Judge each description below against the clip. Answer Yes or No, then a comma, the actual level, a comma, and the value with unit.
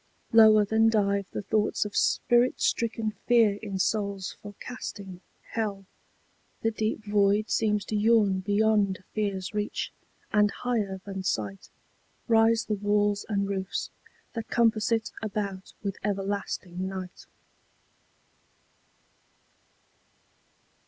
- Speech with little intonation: Yes, narrow, 1.8 semitones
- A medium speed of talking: No, slow, 110 wpm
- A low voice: No, high, 205 Hz